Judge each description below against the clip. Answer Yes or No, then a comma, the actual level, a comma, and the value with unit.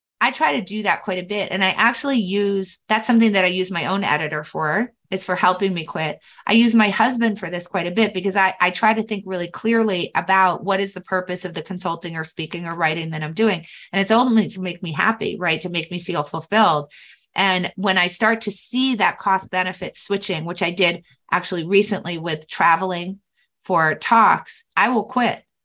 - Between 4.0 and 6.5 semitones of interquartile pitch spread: No, average, 3.4 semitones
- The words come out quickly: Yes, fast, 220 wpm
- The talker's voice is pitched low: No, high, 190 Hz